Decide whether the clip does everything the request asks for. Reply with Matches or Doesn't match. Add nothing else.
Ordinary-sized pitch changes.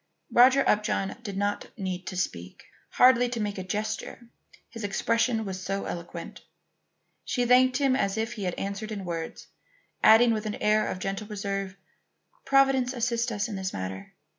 Matches